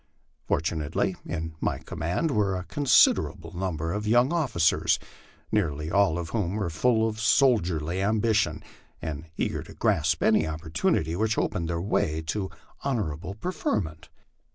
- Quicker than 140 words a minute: No, slow, 135 wpm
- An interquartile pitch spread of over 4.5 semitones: Yes, average, 5.2 semitones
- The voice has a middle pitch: No, very low, 90 Hz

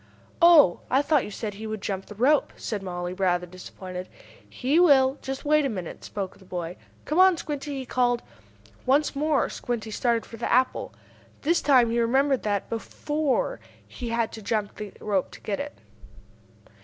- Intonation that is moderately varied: No, wide, 5.9 semitones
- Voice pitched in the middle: No, high, 235 Hz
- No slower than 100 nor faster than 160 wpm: No, average, 180 wpm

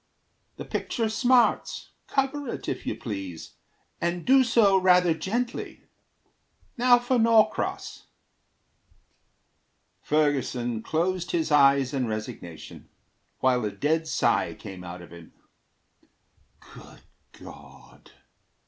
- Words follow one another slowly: Yes, slow, 105 wpm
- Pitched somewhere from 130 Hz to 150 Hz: No, medium, 160 Hz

